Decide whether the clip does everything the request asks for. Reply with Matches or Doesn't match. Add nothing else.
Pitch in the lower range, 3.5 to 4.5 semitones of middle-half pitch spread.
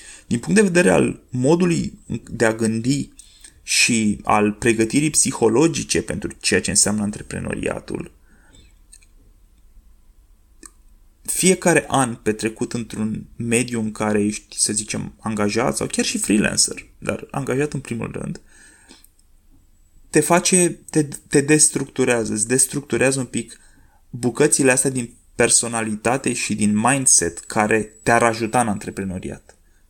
Doesn't match